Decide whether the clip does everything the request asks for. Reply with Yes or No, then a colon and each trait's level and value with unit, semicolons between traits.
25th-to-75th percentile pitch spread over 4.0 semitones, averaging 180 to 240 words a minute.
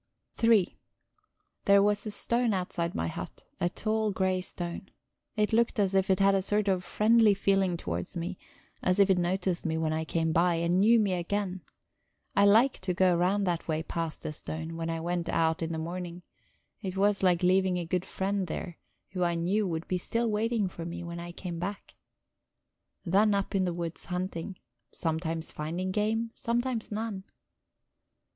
No: average, 3.1 semitones; average, 185 wpm